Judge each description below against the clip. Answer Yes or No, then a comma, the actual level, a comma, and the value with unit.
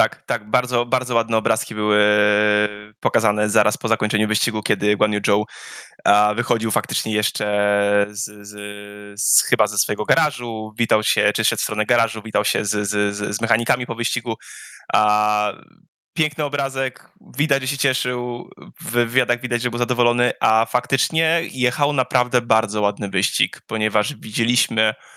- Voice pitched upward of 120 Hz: No, low, 110 Hz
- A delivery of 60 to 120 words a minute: No, average, 145 wpm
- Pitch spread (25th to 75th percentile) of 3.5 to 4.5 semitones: No, average, 2.7 semitones